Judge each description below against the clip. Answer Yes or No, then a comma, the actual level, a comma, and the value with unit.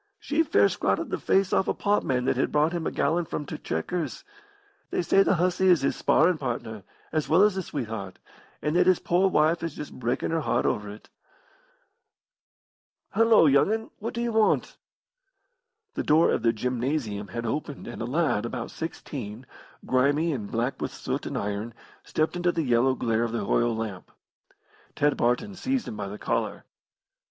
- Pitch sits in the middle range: Yes, medium, 145 Hz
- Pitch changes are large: Yes, wide, 7.0 semitones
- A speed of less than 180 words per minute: No, average, 185 wpm